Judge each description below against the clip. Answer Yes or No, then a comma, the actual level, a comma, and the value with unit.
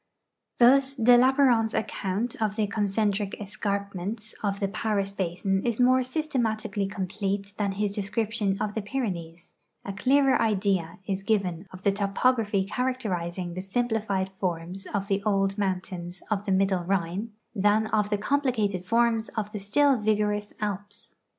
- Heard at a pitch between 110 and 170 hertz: No, high, 205 Hz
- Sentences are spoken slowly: No, average, 145 wpm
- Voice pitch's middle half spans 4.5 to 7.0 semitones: No, narrow, 2.4 semitones